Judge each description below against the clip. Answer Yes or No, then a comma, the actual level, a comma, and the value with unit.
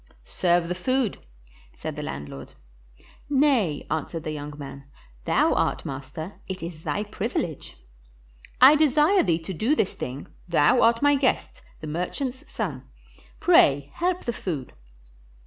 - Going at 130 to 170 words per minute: Yes, average, 140 wpm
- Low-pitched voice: No, medium, 180 Hz